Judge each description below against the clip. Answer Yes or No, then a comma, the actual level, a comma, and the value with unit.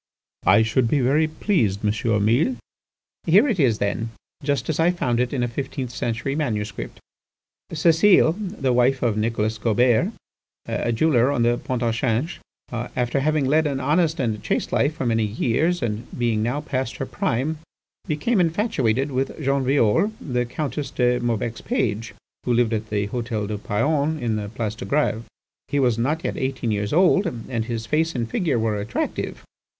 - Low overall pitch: Yes, low, 125 Hz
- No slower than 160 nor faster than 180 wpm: Yes, average, 175 wpm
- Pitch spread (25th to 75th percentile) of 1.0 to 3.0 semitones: No, average, 4.8 semitones